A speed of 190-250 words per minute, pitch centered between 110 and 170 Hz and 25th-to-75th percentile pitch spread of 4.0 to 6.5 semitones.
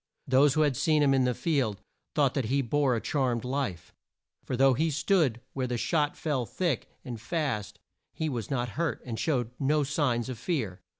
No: average, 195 wpm; low, 135 Hz; average, 3.6 semitones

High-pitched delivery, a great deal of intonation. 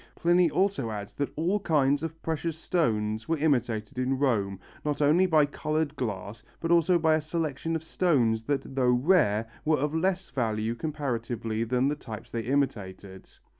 No: medium, 140 Hz; wide, 6.0 semitones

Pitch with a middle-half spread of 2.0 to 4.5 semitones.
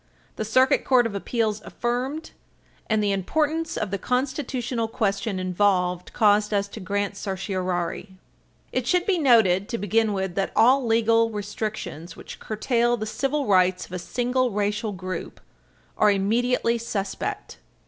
Yes: average, 3.6 semitones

